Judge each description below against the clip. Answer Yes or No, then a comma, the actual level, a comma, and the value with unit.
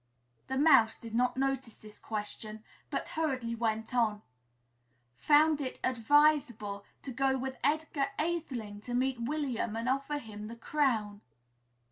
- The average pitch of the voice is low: No, high, 245 Hz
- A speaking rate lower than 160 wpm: Yes, average, 140 wpm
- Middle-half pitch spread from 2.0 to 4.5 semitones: Yes, average, 4.2 semitones